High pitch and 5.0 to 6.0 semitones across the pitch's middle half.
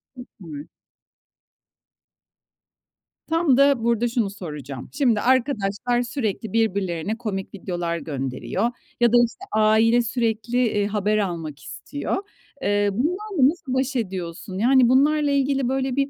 Yes: high, 230 Hz; average, 5.3 semitones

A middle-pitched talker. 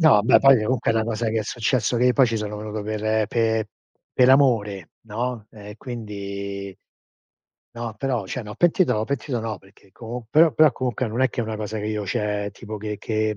No: low, 110 Hz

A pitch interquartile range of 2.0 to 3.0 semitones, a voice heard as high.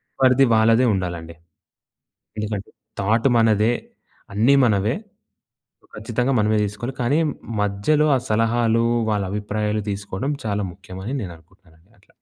No: average, 2.7 semitones; low, 105 Hz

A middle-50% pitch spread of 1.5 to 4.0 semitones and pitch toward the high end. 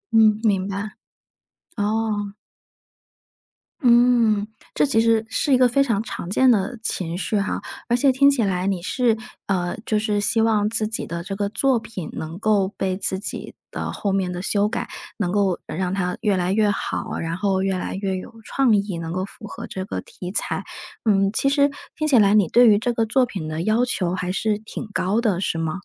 Yes: average, 3.2 semitones; high, 205 Hz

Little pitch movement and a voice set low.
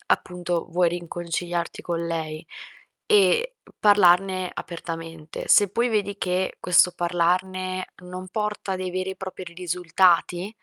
No: narrow, 1.7 semitones; medium, 180 Hz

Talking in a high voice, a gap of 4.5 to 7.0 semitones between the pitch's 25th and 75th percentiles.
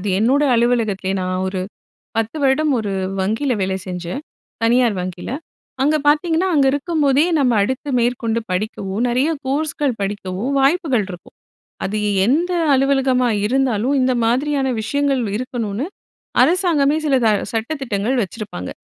Yes: very high, 250 Hz; average, 5.1 semitones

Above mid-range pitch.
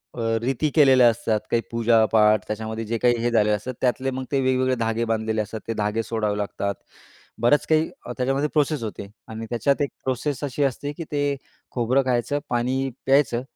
No: low, 120 Hz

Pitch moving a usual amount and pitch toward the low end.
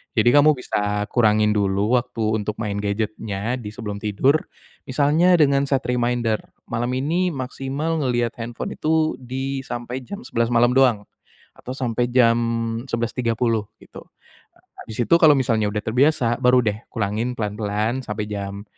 Yes: average, 3.5 semitones; low, 120 Hz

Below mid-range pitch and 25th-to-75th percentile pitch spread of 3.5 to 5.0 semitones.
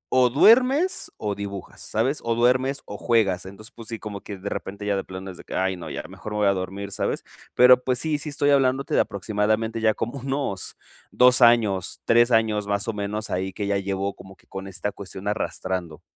Yes: low, 105 Hz; average, 4.1 semitones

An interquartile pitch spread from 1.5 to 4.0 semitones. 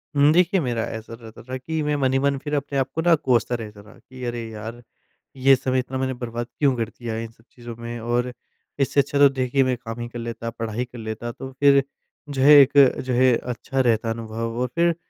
Yes: average, 2.9 semitones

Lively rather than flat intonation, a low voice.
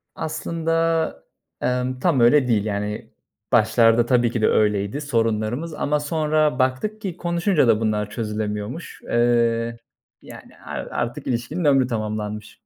Yes: wide, 5.8 semitones; low, 120 Hz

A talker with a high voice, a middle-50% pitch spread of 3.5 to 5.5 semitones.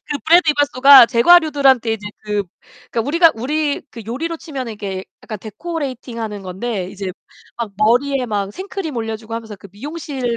Yes: high, 240 Hz; average, 5.2 semitones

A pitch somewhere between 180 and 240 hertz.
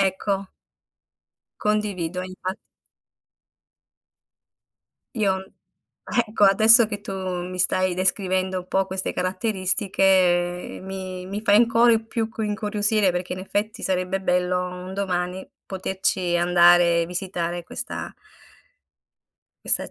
Yes: high, 190 Hz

